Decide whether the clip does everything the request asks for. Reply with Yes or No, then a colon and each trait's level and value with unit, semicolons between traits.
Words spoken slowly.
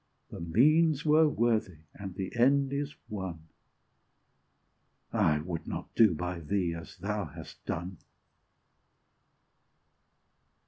Yes: slow, 105 wpm